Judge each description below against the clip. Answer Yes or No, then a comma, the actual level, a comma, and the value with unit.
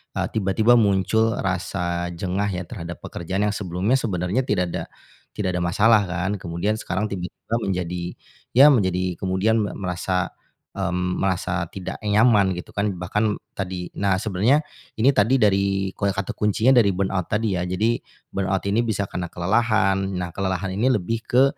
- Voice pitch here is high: No, very low, 95 Hz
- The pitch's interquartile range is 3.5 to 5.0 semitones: No, average, 2.9 semitones